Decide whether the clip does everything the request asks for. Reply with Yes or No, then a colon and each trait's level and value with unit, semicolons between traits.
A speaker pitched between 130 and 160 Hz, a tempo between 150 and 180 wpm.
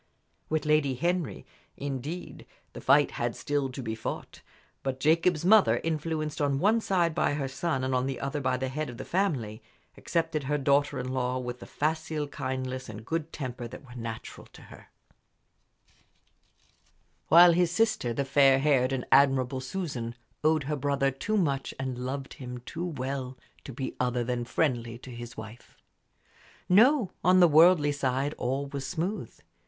Yes: medium, 140 Hz; average, 170 wpm